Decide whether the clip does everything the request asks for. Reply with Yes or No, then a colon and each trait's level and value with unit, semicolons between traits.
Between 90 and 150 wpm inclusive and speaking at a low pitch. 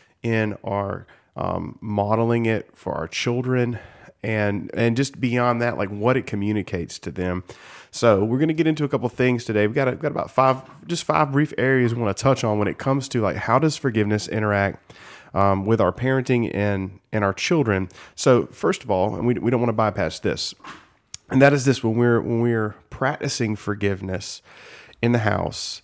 No: average, 200 wpm; low, 115 Hz